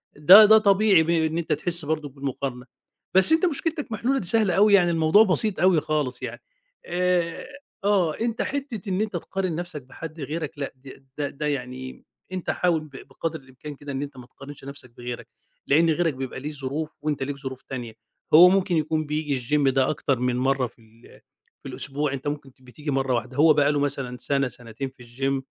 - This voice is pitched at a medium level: Yes, medium, 150 Hz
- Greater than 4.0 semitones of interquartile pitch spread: Yes, average, 4.7 semitones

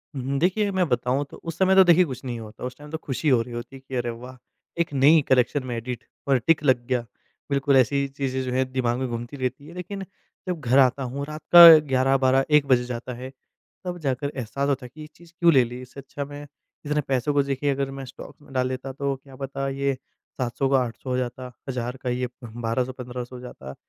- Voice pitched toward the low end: Yes, low, 130 Hz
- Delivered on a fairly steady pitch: Yes, narrow, 2.2 semitones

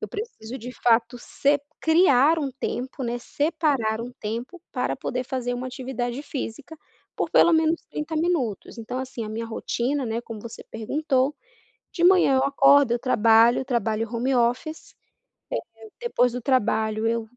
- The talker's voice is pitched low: No, very high, 250 Hz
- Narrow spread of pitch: No, average, 3.8 semitones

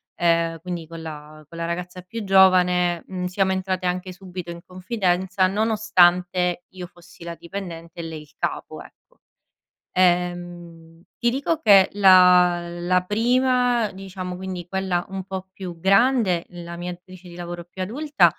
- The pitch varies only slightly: Yes, narrow, 1.7 semitones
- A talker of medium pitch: Yes, medium, 180 Hz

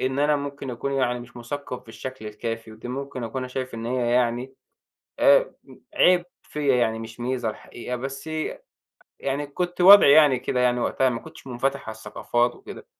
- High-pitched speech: No, low, 130 Hz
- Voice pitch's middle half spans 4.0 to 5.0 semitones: No, average, 2.8 semitones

